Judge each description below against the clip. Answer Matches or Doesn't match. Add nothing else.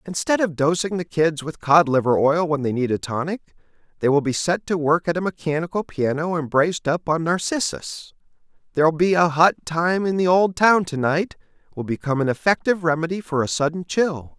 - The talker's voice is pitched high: Doesn't match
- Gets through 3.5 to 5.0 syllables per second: Doesn't match